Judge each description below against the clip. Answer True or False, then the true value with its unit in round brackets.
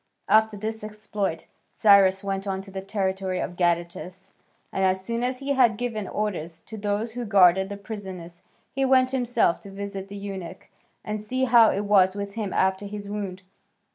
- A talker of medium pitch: False (200 Hz)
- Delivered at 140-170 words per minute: False (180 wpm)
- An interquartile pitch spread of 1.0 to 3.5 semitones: True (2.4 semitones)